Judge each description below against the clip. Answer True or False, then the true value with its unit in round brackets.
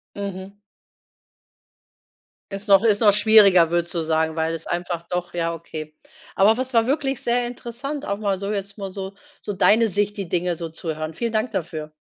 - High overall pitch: True (195 Hz)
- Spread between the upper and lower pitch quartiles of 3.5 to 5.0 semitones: True (4.3 semitones)